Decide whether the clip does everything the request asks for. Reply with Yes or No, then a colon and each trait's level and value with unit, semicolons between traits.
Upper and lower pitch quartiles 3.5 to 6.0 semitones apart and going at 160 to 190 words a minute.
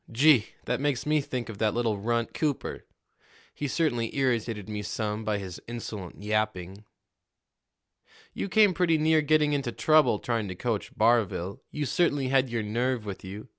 Yes: average, 5.3 semitones; average, 165 wpm